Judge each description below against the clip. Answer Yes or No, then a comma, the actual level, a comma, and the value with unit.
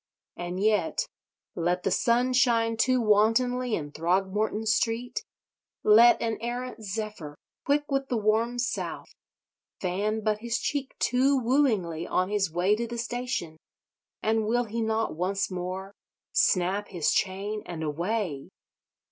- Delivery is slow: Yes, slow, 130 wpm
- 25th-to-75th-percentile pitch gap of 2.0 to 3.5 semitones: No, average, 4.3 semitones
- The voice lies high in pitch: Yes, high, 215 Hz